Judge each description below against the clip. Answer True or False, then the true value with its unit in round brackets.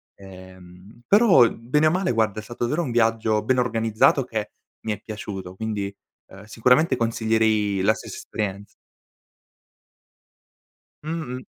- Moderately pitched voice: False (110 Hz)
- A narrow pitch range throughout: False (3.4 semitones)